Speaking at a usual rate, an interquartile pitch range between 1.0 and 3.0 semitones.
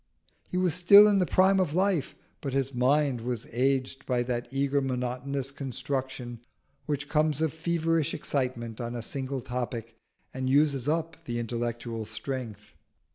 No: average, 150 wpm; average, 3.9 semitones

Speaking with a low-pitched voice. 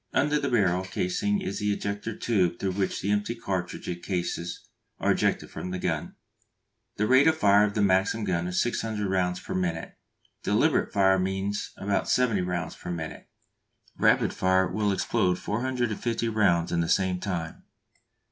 Yes: low, 100 Hz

